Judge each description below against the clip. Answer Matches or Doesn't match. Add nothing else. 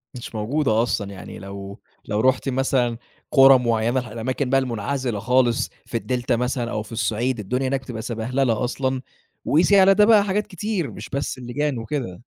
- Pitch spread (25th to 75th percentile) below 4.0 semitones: Matches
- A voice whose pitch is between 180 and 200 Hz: Doesn't match